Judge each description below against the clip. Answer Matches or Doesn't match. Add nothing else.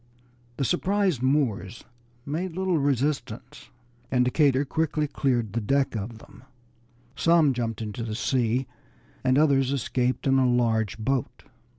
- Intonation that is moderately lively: Matches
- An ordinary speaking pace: Doesn't match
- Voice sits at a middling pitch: Doesn't match